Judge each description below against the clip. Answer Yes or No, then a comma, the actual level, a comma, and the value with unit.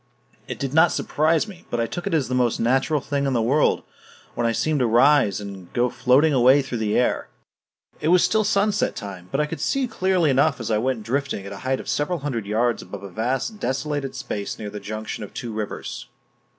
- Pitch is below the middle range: Yes, low, 130 Hz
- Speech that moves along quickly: Yes, fast, 225 wpm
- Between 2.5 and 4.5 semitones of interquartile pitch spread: No, average, 5.3 semitones